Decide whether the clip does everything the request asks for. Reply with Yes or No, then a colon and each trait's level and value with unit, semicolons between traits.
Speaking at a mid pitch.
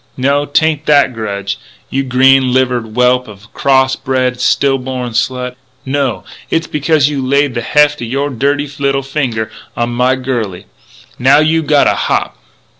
No: low, 130 Hz